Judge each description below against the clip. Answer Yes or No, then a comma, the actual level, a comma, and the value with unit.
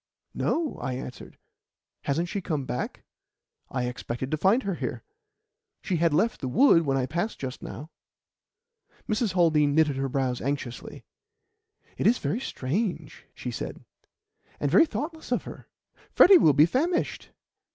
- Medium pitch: Yes, medium, 155 Hz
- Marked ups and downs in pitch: Yes, wide, 8.0 semitones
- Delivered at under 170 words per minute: Yes, average, 150 wpm